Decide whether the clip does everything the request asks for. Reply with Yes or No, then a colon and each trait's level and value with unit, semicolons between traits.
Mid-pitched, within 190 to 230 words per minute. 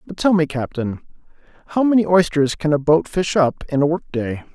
Yes: medium, 160 Hz; average, 200 wpm